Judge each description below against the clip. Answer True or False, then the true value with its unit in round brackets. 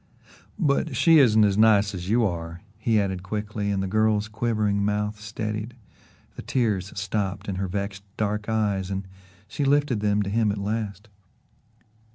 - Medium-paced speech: True (165 wpm)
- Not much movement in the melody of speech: True (1.8 semitones)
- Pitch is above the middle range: False (105 Hz)